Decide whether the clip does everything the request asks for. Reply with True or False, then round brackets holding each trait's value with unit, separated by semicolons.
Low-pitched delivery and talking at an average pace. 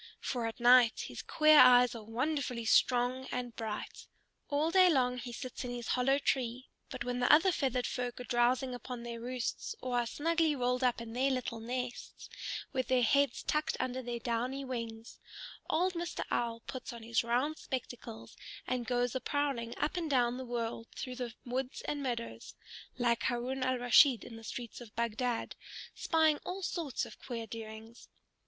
False (250 Hz; 180 wpm)